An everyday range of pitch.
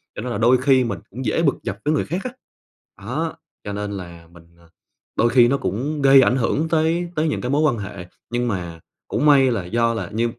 No: wide, 5.9 semitones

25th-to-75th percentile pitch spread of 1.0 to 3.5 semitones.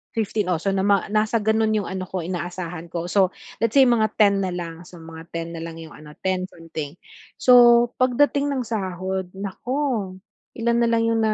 No: average, 4.3 semitones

